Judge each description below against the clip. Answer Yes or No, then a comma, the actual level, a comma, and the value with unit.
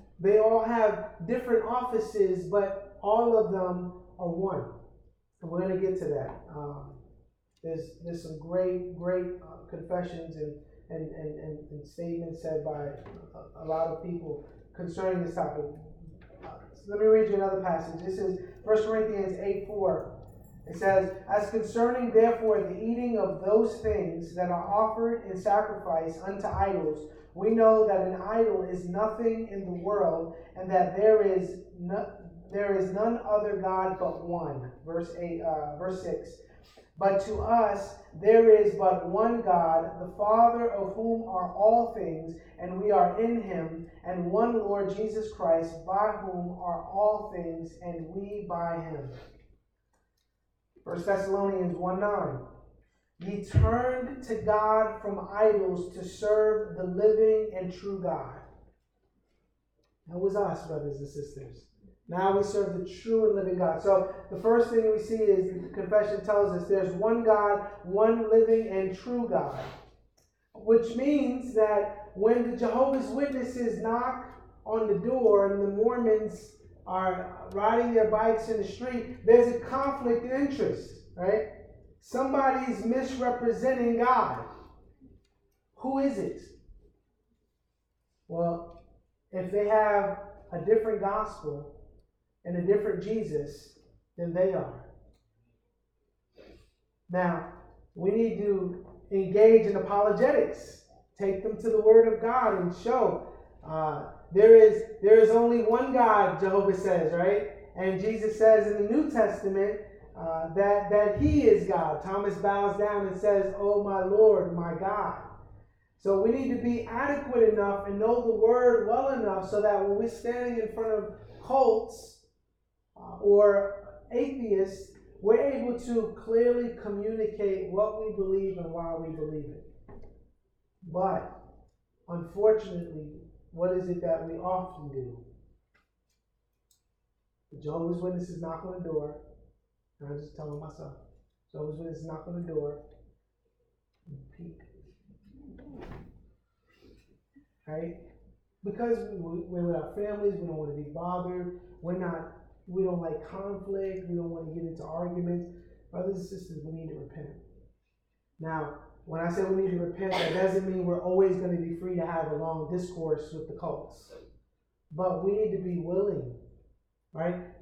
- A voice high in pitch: Yes, high, 195 Hz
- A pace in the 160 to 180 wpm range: No, average, 150 wpm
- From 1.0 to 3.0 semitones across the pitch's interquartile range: No, average, 4.2 semitones